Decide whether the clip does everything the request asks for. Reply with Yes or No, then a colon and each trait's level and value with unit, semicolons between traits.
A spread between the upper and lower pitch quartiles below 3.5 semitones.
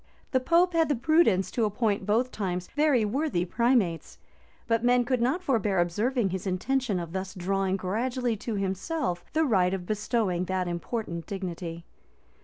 No: wide, 5.5 semitones